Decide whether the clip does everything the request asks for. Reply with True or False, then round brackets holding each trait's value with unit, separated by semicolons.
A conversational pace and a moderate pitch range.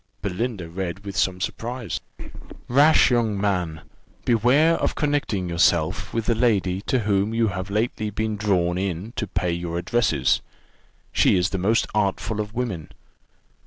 True (150 wpm; 4.2 semitones)